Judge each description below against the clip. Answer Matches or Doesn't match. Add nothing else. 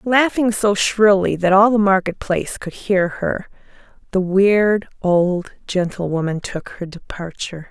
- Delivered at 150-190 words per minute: Doesn't match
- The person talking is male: Doesn't match